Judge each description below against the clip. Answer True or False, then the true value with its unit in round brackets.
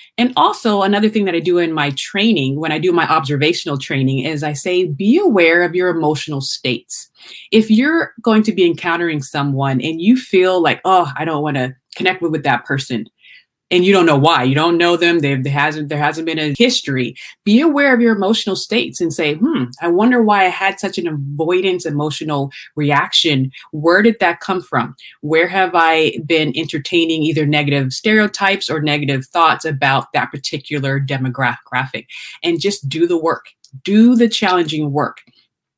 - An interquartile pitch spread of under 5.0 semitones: True (4.5 semitones)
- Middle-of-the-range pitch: True (165 Hz)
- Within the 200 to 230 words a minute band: False (185 wpm)